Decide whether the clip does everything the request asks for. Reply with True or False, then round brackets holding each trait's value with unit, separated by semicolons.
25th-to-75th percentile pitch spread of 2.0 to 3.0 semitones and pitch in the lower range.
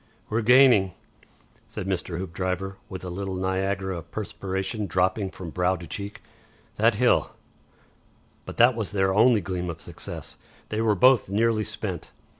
True (2.5 semitones; 95 Hz)